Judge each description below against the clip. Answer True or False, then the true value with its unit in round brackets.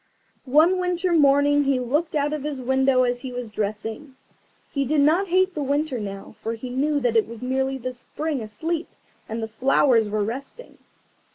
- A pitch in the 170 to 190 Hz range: False (265 Hz)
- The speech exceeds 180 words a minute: True (190 wpm)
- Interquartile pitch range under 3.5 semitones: False (4.0 semitones)